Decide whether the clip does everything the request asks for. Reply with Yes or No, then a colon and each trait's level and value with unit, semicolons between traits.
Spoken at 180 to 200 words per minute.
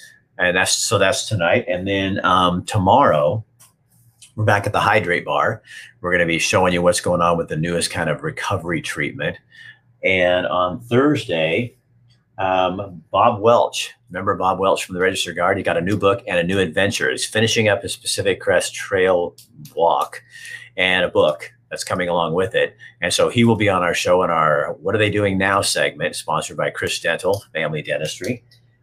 Yes: average, 190 wpm